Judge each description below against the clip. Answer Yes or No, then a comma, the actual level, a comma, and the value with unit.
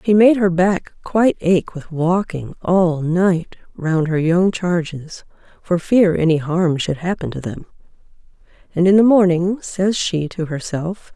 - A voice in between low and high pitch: Yes, medium, 175 Hz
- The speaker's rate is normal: Yes, average, 160 wpm